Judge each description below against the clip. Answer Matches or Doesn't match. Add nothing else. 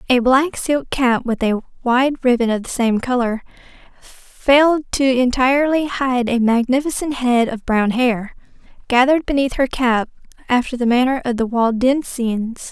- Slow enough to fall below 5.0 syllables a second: Matches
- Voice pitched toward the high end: Matches